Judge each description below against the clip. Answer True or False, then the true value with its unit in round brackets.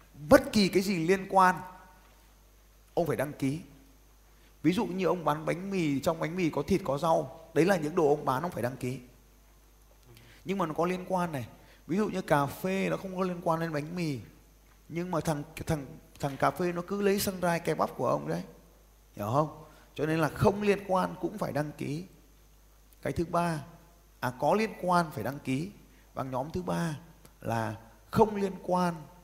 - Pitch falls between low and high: True (165 Hz)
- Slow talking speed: False (205 wpm)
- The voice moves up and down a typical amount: True (4.5 semitones)